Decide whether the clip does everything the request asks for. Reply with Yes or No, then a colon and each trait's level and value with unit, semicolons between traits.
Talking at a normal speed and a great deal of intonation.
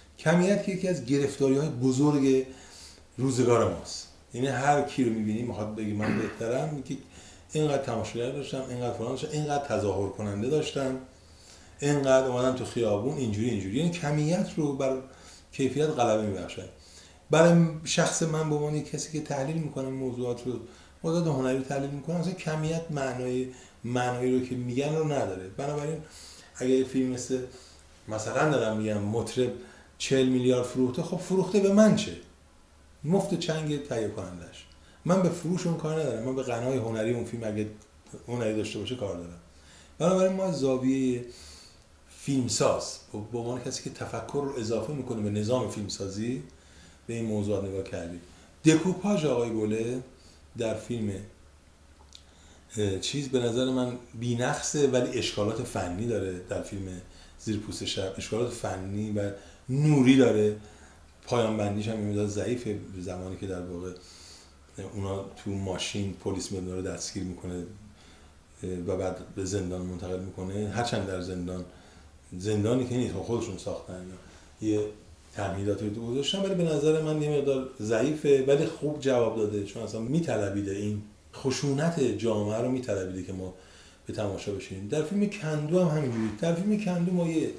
Yes: average, 145 wpm; wide, 6.5 semitones